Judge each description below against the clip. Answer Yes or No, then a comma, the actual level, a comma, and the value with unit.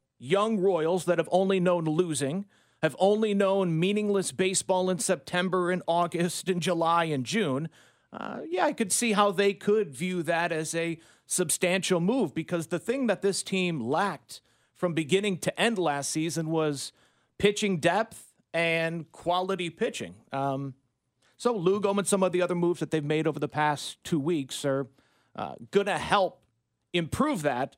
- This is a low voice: No, medium, 180 Hz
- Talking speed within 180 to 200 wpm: No, average, 165 wpm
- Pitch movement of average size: Yes, average, 3.4 semitones